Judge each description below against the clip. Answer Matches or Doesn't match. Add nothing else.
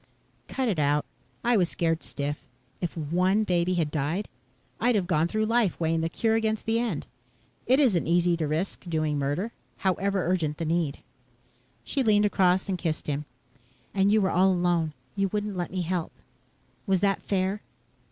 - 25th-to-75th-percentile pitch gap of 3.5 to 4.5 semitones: Matches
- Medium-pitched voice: Matches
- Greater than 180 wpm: Doesn't match